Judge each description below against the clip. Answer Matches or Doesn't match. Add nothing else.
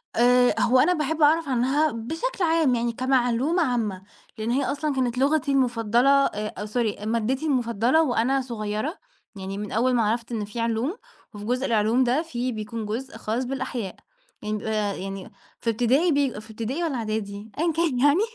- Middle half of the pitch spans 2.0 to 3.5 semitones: Doesn't match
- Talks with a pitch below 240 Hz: Doesn't match